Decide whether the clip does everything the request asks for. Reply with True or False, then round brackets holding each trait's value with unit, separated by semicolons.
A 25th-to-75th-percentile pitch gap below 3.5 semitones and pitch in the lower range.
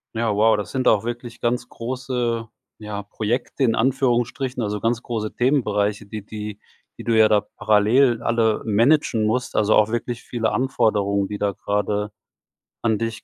True (2.4 semitones; 115 Hz)